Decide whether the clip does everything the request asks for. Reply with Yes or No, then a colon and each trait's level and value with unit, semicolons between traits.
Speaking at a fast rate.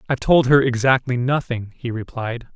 No: average, 165 wpm